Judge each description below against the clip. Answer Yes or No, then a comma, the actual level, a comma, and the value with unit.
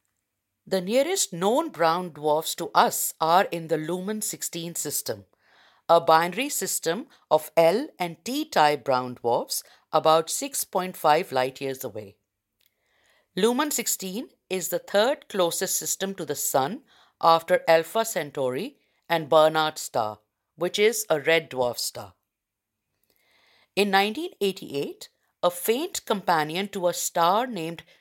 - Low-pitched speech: No, medium, 170 Hz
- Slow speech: Yes, slow, 125 wpm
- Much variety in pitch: No, average, 4.7 semitones